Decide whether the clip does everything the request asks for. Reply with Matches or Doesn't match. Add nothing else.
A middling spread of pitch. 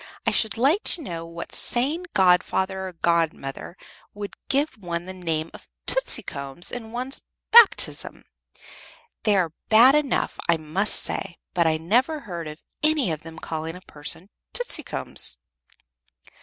Doesn't match